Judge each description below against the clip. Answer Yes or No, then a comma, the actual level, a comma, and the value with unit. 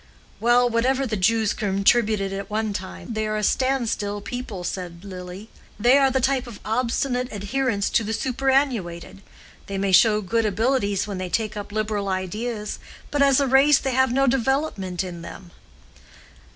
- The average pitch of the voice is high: Yes, high, 220 Hz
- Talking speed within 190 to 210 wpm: No, average, 170 wpm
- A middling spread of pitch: Yes, average, 4.3 semitones